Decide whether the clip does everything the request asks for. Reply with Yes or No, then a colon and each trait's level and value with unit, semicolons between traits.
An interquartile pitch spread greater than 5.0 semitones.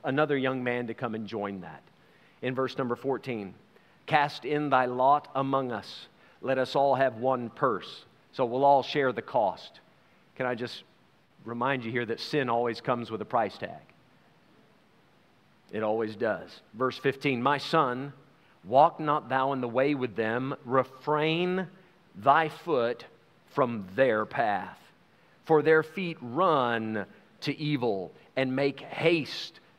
No: average, 3.3 semitones